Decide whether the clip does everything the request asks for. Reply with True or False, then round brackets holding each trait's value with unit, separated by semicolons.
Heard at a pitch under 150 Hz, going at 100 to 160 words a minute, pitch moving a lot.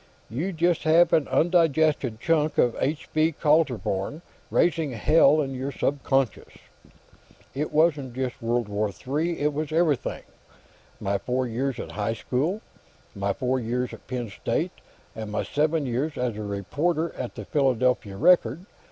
False (135 Hz; 150 wpm; 4.8 semitones)